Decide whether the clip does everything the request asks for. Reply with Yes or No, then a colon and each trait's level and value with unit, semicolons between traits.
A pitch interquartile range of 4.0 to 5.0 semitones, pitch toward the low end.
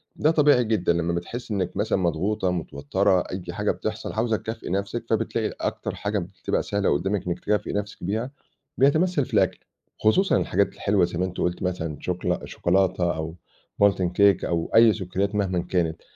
No: average, 3.6 semitones; low, 100 Hz